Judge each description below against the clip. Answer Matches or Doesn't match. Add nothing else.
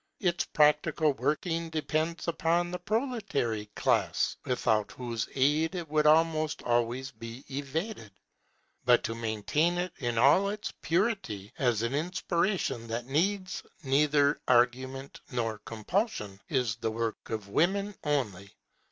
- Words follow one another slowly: Matches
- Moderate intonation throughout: Doesn't match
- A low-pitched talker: Doesn't match